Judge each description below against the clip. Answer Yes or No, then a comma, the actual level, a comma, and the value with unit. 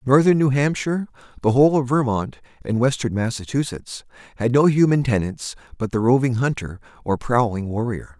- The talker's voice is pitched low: Yes, low, 125 Hz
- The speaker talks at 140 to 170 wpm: Yes, average, 155 wpm